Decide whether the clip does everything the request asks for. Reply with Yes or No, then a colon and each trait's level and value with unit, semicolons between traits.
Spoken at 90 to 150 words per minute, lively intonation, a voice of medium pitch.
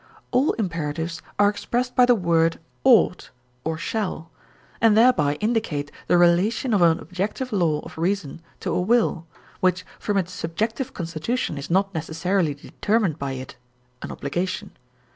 No: average, 145 wpm; average, 4.8 semitones; medium, 180 Hz